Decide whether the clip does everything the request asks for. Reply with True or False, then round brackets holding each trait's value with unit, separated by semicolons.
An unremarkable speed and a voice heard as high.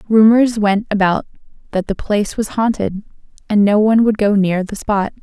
True (185 wpm; 210 Hz)